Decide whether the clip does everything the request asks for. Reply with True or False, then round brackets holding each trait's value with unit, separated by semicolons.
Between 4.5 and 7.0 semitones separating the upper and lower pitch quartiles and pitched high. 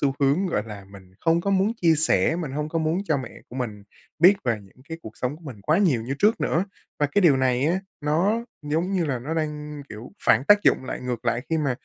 False (5.1 semitones; 150 Hz)